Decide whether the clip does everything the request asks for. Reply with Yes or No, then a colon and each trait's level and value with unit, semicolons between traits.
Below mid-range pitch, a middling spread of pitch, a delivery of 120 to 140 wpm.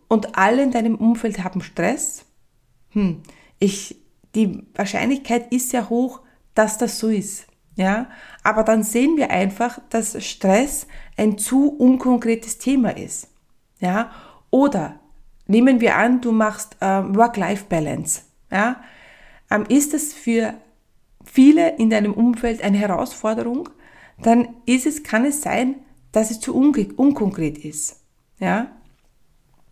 No: high, 230 Hz; average, 3.6 semitones; average, 130 wpm